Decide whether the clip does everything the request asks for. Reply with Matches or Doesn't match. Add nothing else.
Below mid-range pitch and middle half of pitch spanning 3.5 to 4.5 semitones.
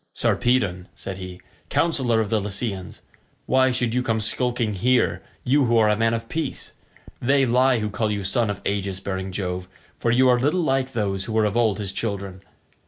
Matches